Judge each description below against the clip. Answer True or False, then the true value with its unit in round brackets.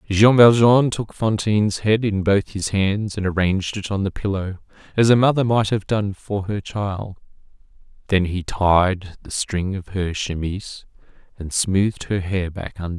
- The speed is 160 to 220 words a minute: True (185 wpm)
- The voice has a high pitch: False (100 Hz)